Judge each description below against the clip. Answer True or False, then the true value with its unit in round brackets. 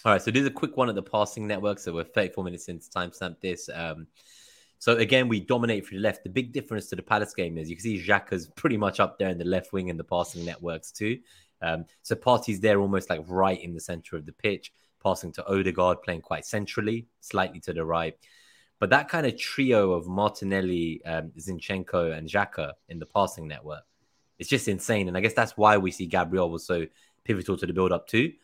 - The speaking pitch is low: True (95 Hz)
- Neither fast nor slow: False (230 wpm)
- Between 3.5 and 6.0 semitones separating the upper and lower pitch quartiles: True (4.0 semitones)